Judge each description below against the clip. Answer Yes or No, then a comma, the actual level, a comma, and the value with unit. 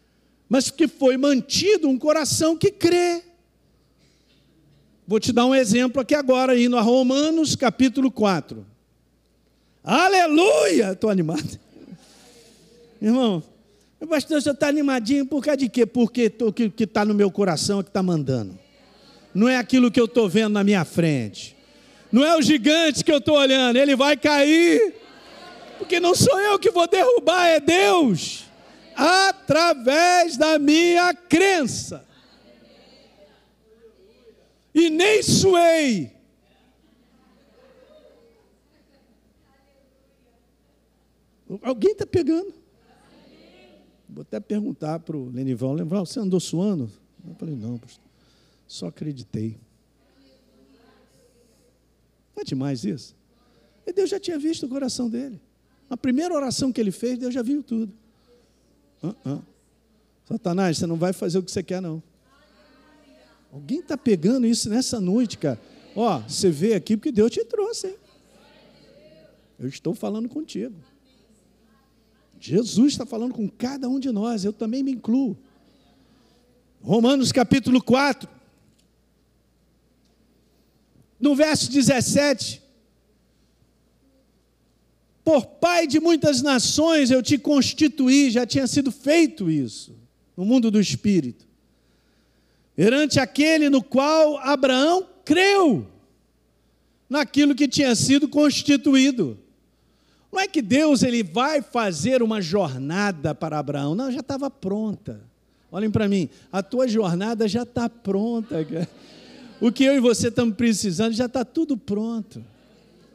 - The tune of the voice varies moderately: No, wide, 6.7 semitones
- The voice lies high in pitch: Yes, high, 245 Hz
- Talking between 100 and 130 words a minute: Yes, average, 125 wpm